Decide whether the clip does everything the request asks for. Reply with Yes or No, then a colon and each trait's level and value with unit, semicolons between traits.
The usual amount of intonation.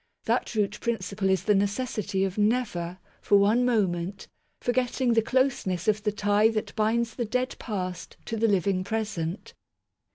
Yes: average, 3.2 semitones